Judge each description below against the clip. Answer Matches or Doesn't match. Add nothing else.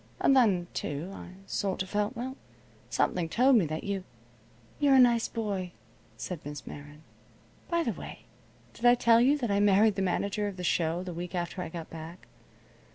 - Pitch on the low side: Doesn't match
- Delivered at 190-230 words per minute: Matches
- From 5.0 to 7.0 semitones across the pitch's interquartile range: Matches